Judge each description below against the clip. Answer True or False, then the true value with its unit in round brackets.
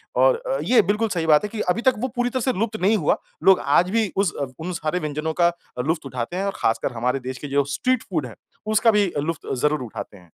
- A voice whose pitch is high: False (180 Hz)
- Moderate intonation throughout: False (6.9 semitones)